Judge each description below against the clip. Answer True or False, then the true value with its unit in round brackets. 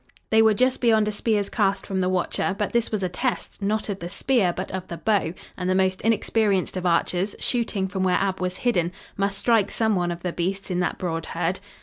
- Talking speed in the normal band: False (235 wpm)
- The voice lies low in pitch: False (195 Hz)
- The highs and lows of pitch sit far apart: False (3.0 semitones)